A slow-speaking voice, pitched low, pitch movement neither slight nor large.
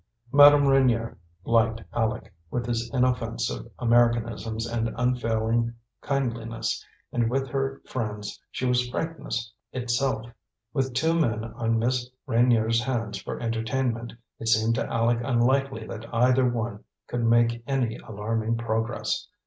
No: slow, 125 wpm; low, 115 Hz; narrow, 1.9 semitones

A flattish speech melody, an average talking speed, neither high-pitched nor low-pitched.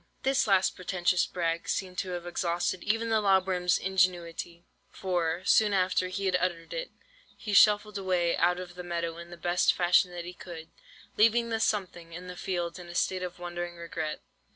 Yes: narrow, 1.8 semitones; average, 190 wpm; medium, 180 Hz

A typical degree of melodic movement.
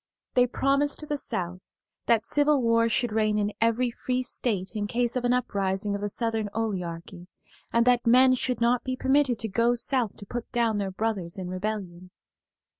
Yes: average, 3.5 semitones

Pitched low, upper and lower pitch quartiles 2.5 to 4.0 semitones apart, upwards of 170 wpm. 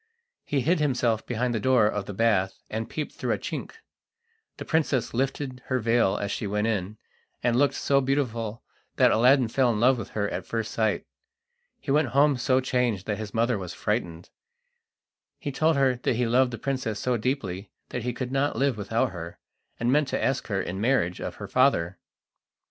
Yes: low, 120 Hz; average, 3.7 semitones; average, 195 wpm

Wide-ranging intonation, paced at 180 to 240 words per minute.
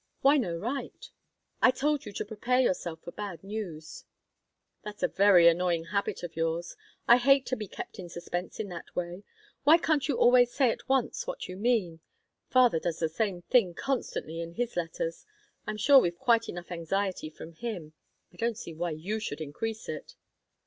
Yes: wide, 6.1 semitones; average, 185 wpm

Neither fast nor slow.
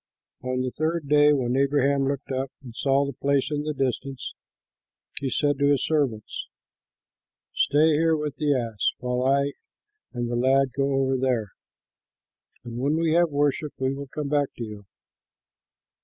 Yes: average, 160 wpm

